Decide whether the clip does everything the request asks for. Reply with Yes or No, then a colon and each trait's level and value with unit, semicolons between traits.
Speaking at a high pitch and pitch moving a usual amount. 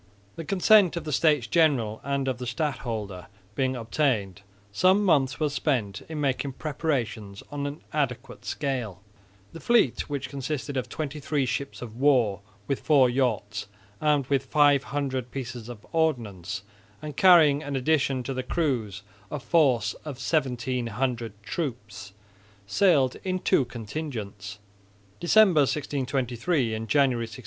No: low, 135 Hz; average, 4.4 semitones